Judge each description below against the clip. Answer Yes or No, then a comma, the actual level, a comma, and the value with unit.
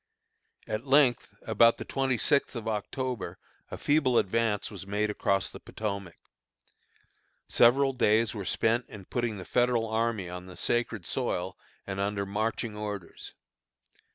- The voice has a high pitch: No, low, 110 Hz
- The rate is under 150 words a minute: Yes, average, 140 wpm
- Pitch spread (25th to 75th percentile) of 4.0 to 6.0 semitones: No, average, 3.3 semitones